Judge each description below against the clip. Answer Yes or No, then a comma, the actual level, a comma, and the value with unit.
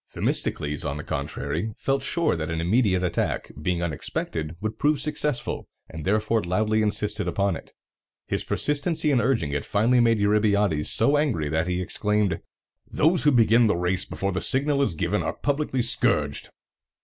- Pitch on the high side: No, low, 105 Hz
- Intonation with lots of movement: Yes, wide, 7.0 semitones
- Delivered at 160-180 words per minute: Yes, average, 165 wpm